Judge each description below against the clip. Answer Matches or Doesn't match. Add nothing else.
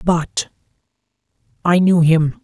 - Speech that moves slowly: Matches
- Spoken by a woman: Doesn't match